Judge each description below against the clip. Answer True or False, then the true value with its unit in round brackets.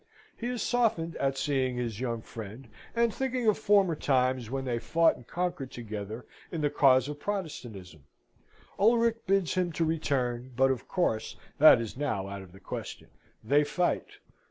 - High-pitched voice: False (135 Hz)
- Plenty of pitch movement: True (7.0 semitones)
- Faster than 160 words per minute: True (170 wpm)